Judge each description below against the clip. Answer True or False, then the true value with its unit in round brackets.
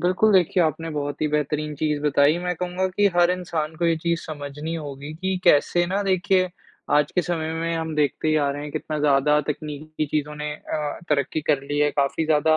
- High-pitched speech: False (155 Hz)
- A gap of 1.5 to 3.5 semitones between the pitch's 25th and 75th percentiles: True (2.7 semitones)